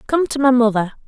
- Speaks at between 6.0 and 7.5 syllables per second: Yes, 6.3 syllables/s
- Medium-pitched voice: No, very high, 250 Hz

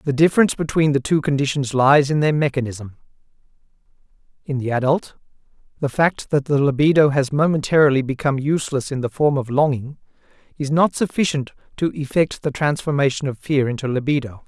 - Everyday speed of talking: Yes, average, 160 wpm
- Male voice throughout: Yes, male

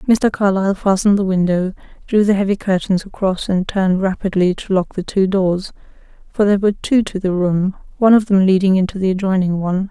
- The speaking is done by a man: No, female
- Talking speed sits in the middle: Yes, average, 195 wpm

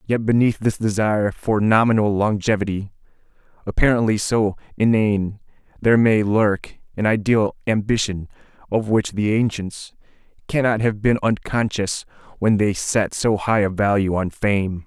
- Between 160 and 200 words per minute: No, slow, 135 wpm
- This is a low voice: Yes, low, 105 Hz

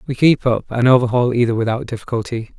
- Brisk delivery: No, average, 185 wpm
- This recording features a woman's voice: No, male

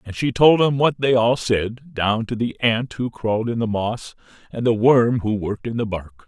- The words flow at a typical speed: No, fast, 240 wpm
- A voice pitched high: No, low, 115 Hz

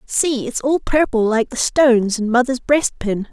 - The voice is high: Yes, very high, 250 Hz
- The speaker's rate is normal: Yes, average, 180 wpm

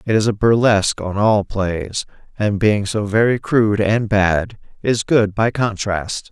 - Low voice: Yes, low, 105 Hz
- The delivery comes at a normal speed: Yes, average, 170 wpm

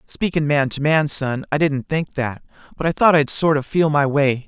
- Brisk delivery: Yes, fast, 240 wpm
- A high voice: No, medium, 145 Hz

